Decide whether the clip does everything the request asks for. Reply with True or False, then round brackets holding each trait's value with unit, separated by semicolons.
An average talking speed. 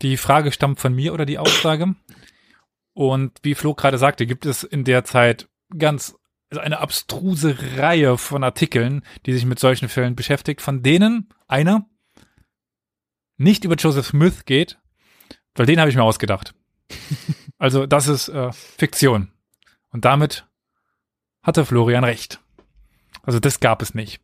True (150 wpm)